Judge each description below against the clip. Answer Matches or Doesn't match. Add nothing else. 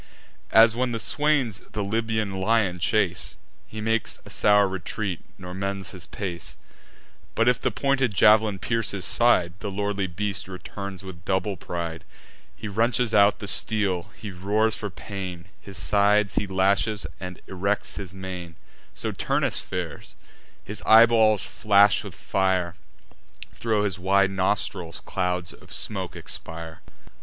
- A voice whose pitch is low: Matches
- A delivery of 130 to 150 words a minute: Matches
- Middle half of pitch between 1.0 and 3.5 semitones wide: Matches